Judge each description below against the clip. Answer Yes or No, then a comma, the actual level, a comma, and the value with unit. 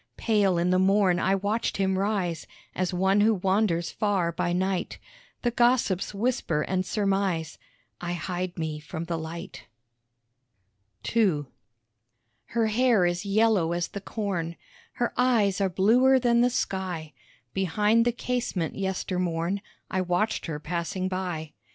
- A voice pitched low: No, high, 190 Hz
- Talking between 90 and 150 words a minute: Yes, average, 140 wpm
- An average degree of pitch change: Yes, average, 3.5 semitones